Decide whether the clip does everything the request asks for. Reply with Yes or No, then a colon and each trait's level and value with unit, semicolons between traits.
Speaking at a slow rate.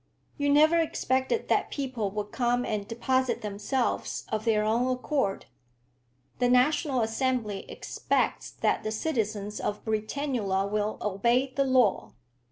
Yes: slow, 130 wpm